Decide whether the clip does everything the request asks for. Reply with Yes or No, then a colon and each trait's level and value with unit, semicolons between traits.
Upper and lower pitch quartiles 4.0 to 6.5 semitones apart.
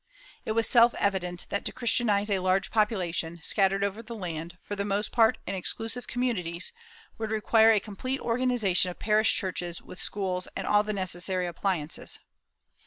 No: average, 3.5 semitones